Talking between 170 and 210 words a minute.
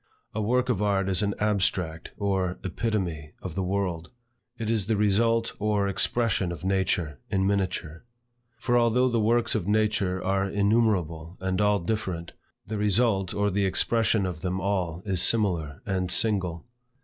No: average, 160 wpm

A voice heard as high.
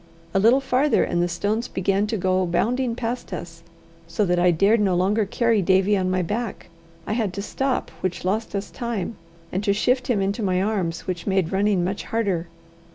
Yes: high, 200 Hz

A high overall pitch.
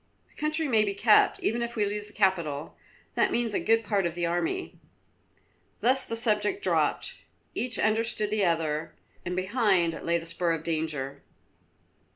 Yes: high, 205 Hz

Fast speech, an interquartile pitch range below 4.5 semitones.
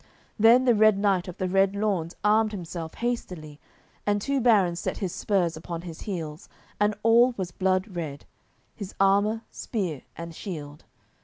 No: average, 160 wpm; average, 3.9 semitones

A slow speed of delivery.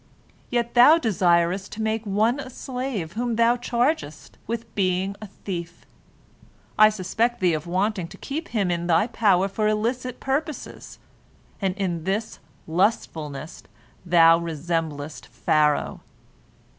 Yes: slow, 130 wpm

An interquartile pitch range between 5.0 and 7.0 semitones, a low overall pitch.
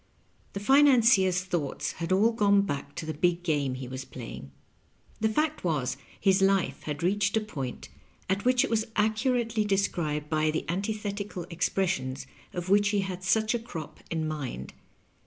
No: wide, 5.4 semitones; high, 190 Hz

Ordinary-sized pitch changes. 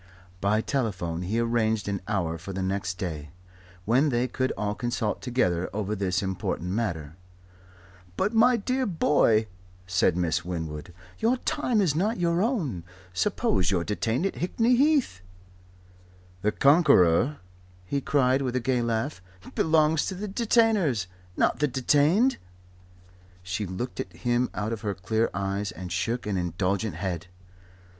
No: wide, 8.2 semitones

